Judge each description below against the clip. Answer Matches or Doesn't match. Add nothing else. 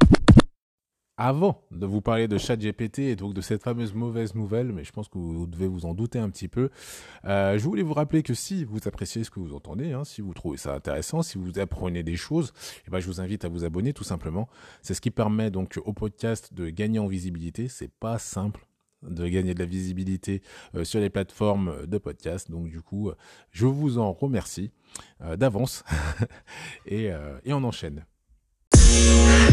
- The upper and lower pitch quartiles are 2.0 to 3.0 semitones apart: Doesn't match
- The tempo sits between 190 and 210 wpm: Matches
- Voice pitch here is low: Matches